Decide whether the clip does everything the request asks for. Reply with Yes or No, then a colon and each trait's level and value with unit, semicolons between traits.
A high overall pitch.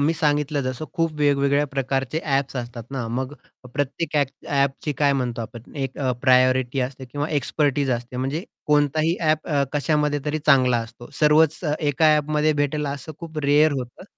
No: medium, 145 Hz